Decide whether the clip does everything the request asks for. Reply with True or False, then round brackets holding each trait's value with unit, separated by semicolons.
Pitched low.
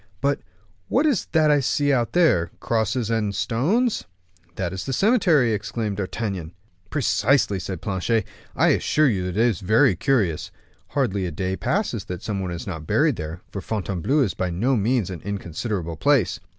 True (110 Hz)